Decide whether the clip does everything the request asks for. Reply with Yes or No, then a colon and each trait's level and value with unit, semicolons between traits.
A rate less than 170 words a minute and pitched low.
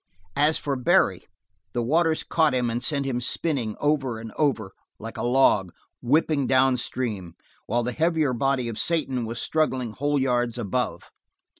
Yes: average, 160 wpm; low, 130 Hz